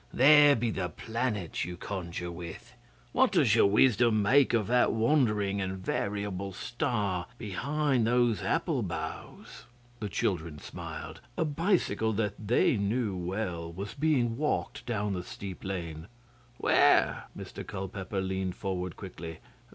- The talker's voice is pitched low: Yes, low, 100 Hz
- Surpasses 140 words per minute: No, slow, 135 wpm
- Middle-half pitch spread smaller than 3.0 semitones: No, average, 4.4 semitones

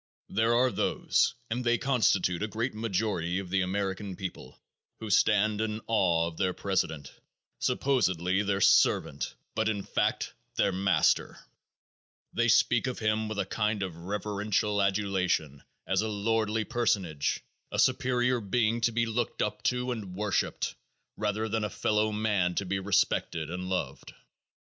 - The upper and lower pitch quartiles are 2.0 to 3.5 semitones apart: Yes, average, 2.9 semitones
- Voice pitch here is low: Yes, low, 105 Hz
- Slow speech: No, average, 150 wpm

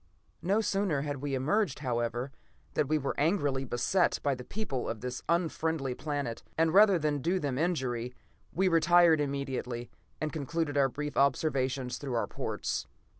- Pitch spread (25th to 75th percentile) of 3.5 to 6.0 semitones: Yes, average, 4.1 semitones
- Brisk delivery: No, average, 160 wpm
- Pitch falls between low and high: Yes, medium, 145 Hz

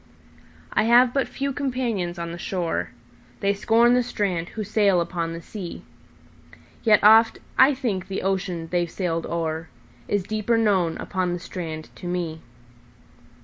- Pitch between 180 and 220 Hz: Yes, medium, 185 Hz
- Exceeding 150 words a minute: No, average, 140 wpm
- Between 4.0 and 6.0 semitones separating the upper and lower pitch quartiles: Yes, average, 4.6 semitones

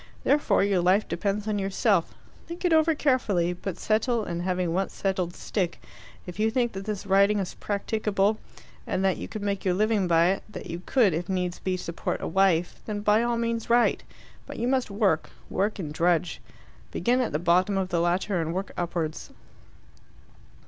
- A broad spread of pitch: No, average, 3.3 semitones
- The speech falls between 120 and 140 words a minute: No, average, 190 wpm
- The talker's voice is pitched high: Yes, high, 195 Hz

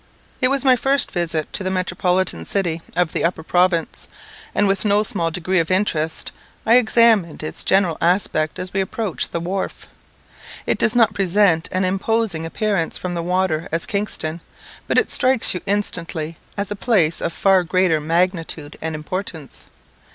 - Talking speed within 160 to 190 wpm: Yes, average, 170 wpm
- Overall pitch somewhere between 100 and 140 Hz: No, medium, 185 Hz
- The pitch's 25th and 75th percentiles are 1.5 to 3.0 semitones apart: No, average, 3.6 semitones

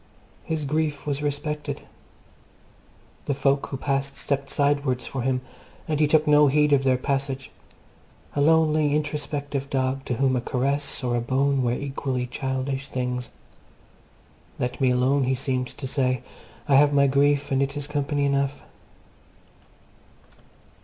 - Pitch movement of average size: No, narrow, 1.7 semitones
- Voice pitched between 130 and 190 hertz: Yes, medium, 140 Hz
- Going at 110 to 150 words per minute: Yes, average, 145 wpm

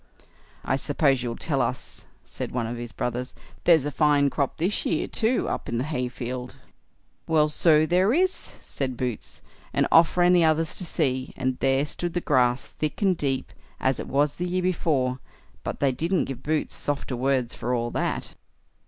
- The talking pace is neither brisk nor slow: Yes, average, 185 wpm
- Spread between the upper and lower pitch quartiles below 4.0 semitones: No, average, 4.3 semitones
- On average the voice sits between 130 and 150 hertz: Yes, medium, 140 Hz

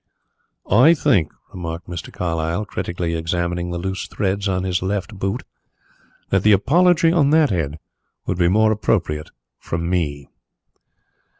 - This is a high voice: No, very low, 90 Hz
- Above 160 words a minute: No, slow, 135 wpm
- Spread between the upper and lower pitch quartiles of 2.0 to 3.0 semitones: No, average, 3.9 semitones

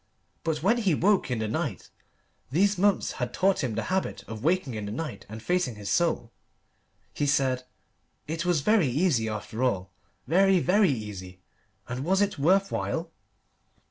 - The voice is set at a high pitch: No, medium, 145 Hz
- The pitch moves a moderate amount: No, wide, 8.5 semitones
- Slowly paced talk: No, average, 170 wpm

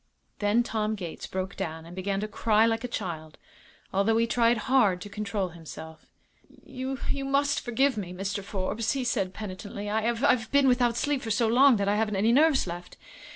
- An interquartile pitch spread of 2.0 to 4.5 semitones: Yes, average, 3.9 semitones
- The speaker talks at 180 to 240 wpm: Yes, average, 195 wpm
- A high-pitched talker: Yes, high, 215 Hz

